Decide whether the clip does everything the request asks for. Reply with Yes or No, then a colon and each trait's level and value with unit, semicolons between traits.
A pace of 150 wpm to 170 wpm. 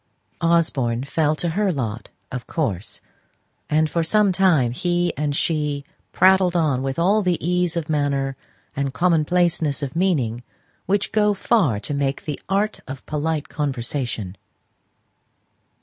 No: slow, 135 wpm